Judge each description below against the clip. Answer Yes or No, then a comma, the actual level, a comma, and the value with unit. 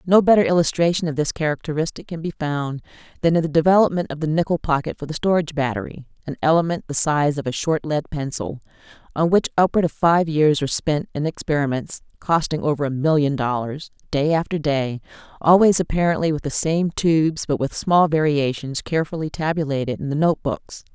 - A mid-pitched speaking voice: Yes, medium, 155 Hz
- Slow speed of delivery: No, average, 185 wpm